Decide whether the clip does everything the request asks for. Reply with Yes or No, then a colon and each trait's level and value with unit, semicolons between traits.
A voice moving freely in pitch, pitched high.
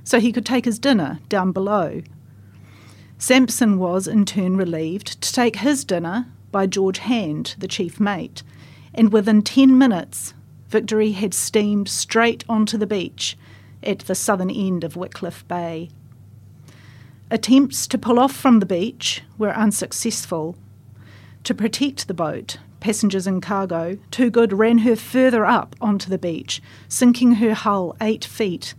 Yes: wide, 6.1 semitones; high, 200 Hz